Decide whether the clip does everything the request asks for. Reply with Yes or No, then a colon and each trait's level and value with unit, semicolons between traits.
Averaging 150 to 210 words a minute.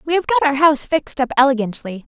No: fast, 225 wpm